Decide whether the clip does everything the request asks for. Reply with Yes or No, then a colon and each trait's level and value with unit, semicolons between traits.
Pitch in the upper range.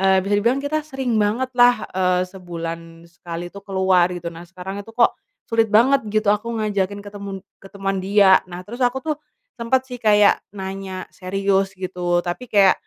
Yes: high, 195 Hz